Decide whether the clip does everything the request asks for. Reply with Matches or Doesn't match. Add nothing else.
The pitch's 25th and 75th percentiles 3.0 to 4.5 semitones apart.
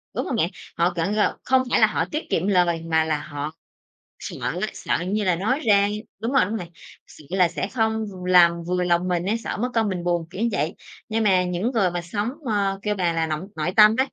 Matches